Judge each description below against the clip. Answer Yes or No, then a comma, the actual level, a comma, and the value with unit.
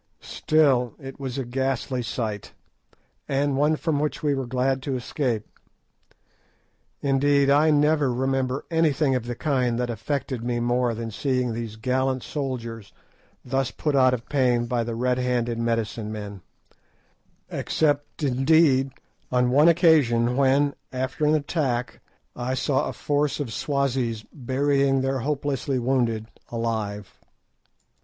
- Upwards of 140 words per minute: No, slow, 135 wpm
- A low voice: Yes, low, 130 Hz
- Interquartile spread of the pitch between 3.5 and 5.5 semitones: No, average, 2.9 semitones